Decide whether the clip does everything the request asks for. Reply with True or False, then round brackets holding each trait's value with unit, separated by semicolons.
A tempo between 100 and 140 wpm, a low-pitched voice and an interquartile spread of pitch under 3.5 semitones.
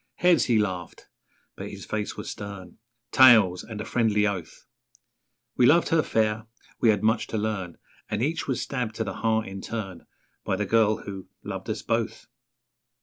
False (175 wpm; 110 Hz; 2.7 semitones)